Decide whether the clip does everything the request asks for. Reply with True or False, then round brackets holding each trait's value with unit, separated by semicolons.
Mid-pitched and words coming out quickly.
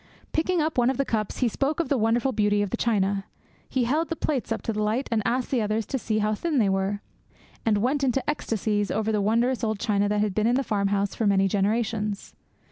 False (220 Hz; 245 wpm)